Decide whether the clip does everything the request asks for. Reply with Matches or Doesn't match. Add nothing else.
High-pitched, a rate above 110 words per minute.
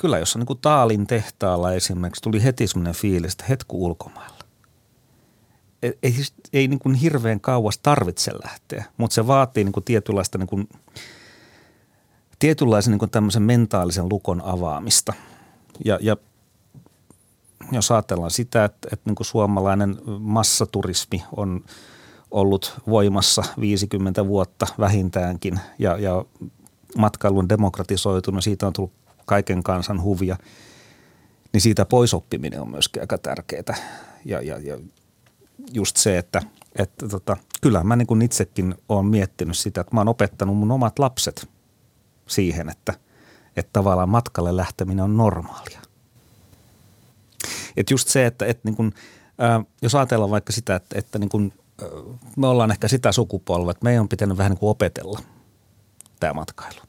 Doesn't match